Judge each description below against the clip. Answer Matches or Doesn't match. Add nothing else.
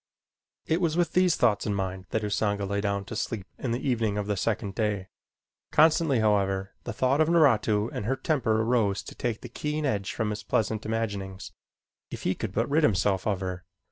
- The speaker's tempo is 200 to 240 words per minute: Matches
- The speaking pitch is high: Doesn't match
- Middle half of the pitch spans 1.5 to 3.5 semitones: Doesn't match